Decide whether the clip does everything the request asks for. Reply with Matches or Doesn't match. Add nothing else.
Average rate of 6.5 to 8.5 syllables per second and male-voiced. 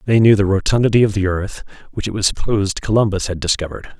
Matches